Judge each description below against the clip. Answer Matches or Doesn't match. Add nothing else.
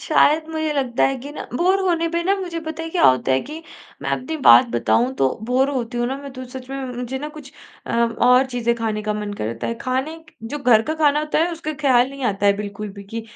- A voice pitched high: Matches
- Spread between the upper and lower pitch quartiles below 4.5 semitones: Doesn't match